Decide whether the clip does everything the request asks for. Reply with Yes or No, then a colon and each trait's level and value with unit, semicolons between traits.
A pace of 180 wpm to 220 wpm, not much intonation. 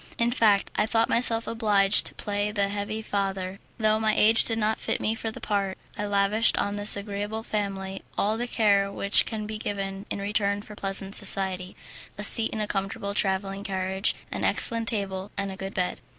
Yes: average, 200 wpm; narrow, 1.7 semitones